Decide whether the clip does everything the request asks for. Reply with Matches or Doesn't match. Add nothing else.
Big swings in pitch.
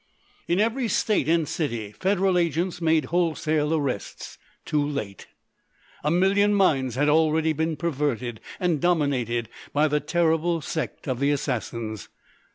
Doesn't match